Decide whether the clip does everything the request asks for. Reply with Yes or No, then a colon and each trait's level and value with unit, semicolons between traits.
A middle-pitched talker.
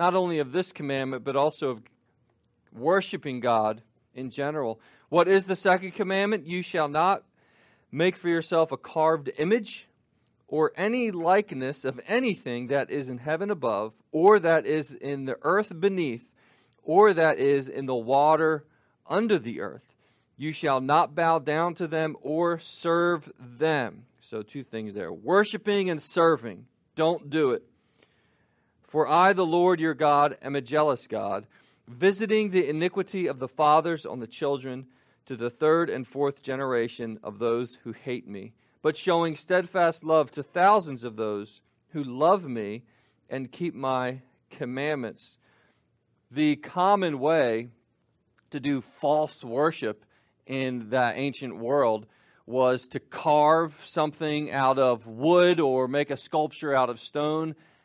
Yes: medium, 150 Hz